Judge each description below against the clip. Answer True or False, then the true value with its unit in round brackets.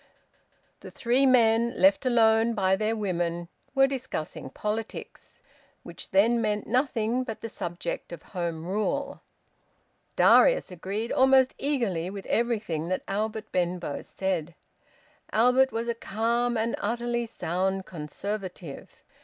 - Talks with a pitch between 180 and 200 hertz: False (220 Hz)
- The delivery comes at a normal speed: False (120 wpm)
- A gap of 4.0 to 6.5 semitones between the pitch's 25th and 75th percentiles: True (4.3 semitones)